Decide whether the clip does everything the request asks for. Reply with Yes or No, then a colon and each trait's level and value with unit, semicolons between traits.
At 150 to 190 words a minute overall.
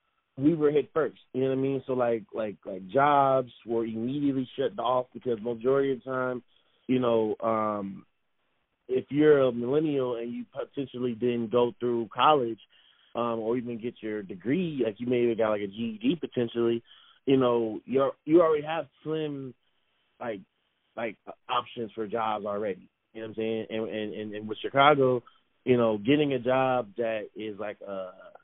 Yes: average, 180 wpm